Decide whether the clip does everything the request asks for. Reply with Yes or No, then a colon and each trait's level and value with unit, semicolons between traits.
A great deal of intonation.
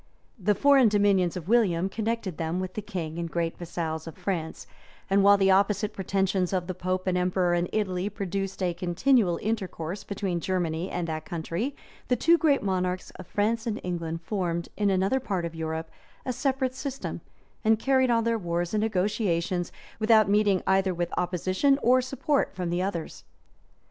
No: average, 3.6 semitones